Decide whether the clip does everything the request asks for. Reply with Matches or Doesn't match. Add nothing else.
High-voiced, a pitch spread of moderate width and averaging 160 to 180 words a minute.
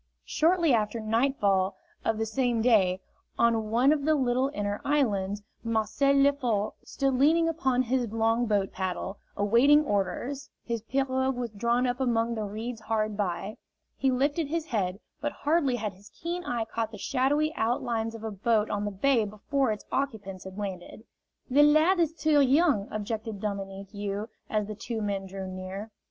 Matches